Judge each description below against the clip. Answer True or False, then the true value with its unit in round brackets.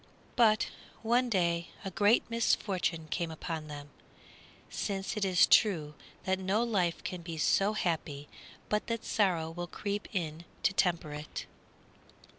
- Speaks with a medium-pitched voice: True (180 Hz)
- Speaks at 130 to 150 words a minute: True (140 wpm)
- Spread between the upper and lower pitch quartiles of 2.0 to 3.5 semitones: False (4.2 semitones)